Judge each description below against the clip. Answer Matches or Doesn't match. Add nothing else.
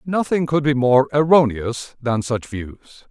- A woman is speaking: Doesn't match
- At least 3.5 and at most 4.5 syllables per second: Matches